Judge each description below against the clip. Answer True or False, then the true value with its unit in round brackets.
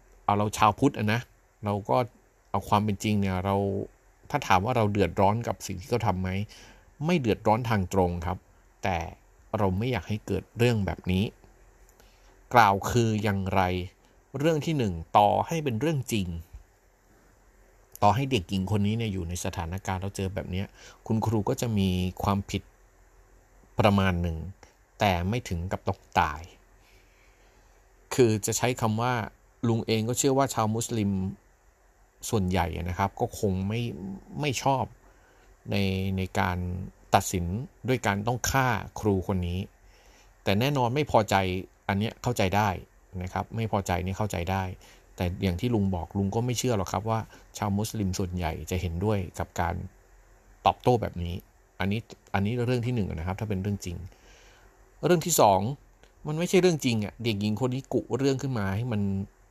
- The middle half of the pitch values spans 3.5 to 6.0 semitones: False (3.1 semitones)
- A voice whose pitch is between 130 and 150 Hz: False (100 Hz)